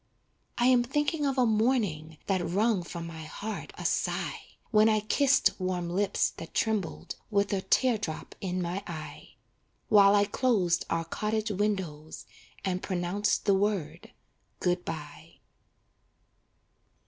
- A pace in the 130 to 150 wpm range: Yes, slow, 135 wpm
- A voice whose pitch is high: Yes, high, 200 Hz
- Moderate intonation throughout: Yes, average, 4.0 semitones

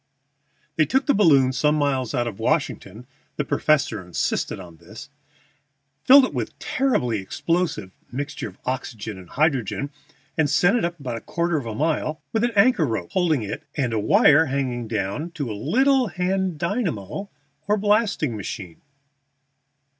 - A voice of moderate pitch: Yes, medium, 145 Hz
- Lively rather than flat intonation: Yes, wide, 8.1 semitones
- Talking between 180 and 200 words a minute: No, average, 160 wpm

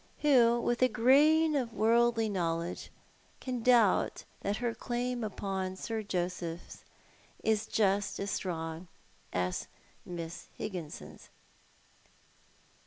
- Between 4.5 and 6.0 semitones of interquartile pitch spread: Yes, average, 5.1 semitones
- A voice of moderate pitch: No, high, 215 Hz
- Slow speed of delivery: Yes, slow, 105 wpm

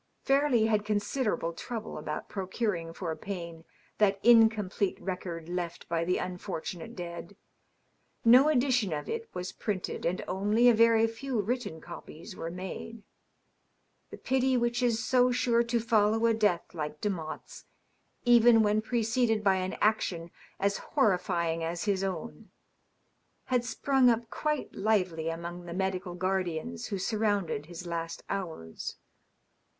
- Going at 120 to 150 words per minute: Yes, slow, 135 wpm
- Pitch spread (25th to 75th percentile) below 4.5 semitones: No, average, 5.0 semitones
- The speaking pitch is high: Yes, high, 200 Hz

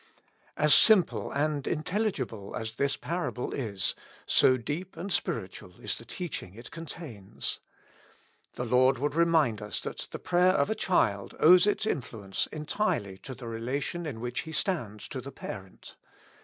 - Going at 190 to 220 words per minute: No, average, 155 wpm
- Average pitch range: No, wide, 7.0 semitones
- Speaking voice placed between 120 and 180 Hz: Yes, low, 135 Hz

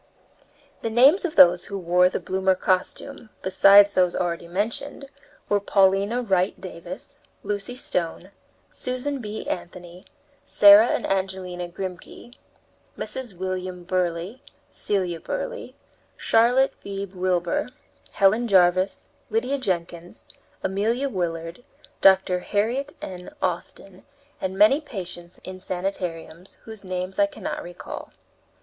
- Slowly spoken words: Yes, slow, 115 wpm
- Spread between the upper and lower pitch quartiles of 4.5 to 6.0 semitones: No, average, 3.8 semitones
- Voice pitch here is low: No, high, 190 Hz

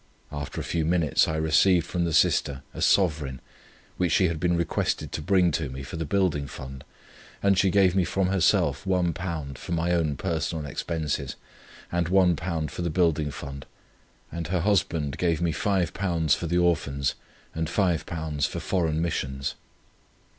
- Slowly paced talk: No, average, 165 wpm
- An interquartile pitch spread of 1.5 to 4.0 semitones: Yes, average, 2.9 semitones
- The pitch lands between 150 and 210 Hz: No, very low, 85 Hz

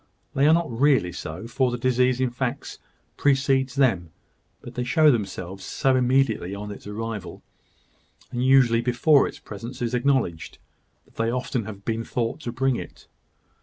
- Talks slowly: No, average, 165 wpm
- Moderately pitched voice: No, low, 125 Hz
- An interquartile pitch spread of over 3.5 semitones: No, average, 2.9 semitones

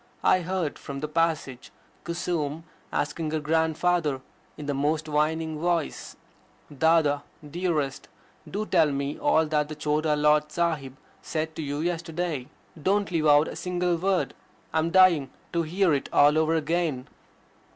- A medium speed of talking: Yes, average, 150 wpm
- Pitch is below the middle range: No, medium, 155 Hz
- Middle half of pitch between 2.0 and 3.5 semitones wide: Yes, narrow, 2.4 semitones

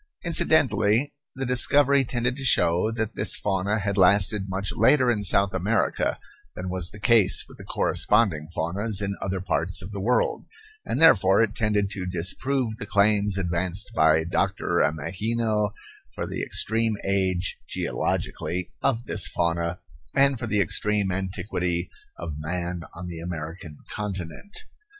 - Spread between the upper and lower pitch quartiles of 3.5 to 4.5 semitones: Yes, average, 3.9 semitones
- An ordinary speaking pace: Yes, average, 145 wpm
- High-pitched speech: No, low, 100 Hz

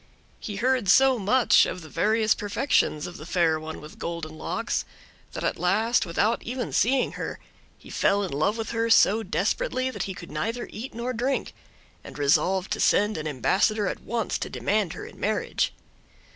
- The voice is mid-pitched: No, high, 210 Hz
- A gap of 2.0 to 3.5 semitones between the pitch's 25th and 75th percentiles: No, average, 5.2 semitones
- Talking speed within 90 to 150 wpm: No, average, 185 wpm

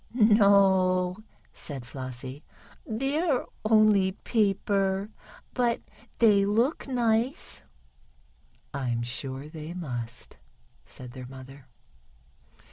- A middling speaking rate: No, slow, 80 wpm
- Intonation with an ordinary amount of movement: No, wide, 8.5 semitones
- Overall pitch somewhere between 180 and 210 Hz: Yes, high, 190 Hz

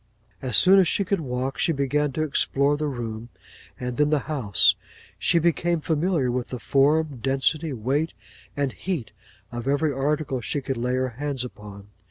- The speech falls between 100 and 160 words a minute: No, average, 175 wpm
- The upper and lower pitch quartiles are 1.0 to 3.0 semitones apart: No, average, 3.5 semitones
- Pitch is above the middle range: No, medium, 140 Hz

